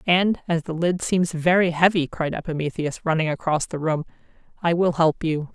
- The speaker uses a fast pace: No, average, 185 wpm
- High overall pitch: No, medium, 165 Hz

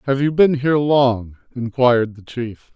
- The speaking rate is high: No, average, 175 wpm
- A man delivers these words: Yes, male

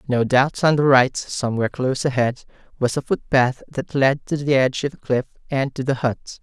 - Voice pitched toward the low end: Yes, low, 130 Hz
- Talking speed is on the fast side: Yes, fast, 215 wpm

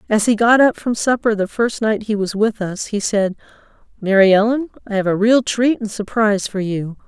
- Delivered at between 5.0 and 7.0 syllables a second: Yes, 5.1 syllables/s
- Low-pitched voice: No, high, 215 Hz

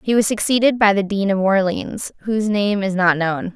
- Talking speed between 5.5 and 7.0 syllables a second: No, 5.1 syllables/s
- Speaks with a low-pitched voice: No, high, 200 Hz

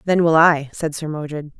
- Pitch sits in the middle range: Yes, medium, 155 Hz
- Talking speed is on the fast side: Yes, fast, 225 wpm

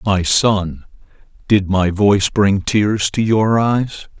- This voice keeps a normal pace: Yes, average, 145 wpm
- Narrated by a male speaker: Yes, male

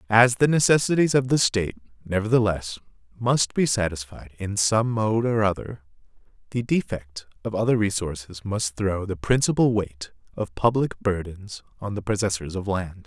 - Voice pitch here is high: No, low, 105 Hz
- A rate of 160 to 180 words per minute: No, average, 150 wpm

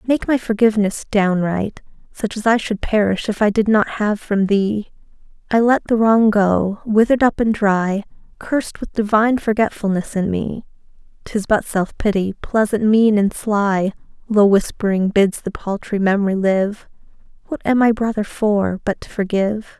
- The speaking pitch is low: No, high, 210 Hz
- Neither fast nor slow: Yes, average, 160 wpm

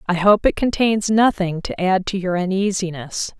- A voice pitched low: No, high, 190 Hz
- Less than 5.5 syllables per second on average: Yes, 4.7 syllables/s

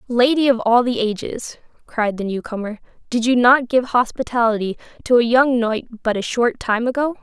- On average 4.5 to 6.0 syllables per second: Yes, 5.2 syllables/s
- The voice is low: No, high, 240 Hz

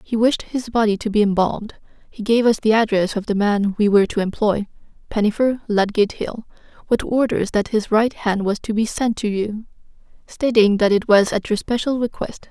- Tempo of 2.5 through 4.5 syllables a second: No, 5.0 syllables/s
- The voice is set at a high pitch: Yes, high, 215 Hz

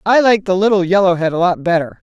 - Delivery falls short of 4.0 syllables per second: No, 6.2 syllables/s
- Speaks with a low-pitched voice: No, high, 190 Hz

